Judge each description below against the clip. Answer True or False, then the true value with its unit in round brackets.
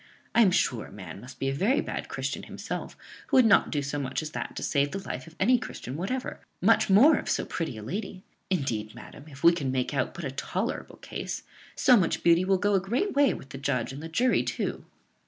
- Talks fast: True (240 wpm)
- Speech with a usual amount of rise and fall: False (6.7 semitones)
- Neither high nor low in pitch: True (165 Hz)